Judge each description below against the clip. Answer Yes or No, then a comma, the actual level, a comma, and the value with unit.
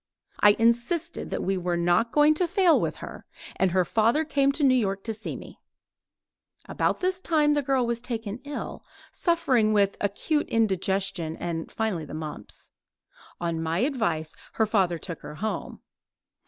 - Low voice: No, high, 220 Hz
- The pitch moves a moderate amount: No, wide, 7.6 semitones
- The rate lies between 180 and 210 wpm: No, average, 165 wpm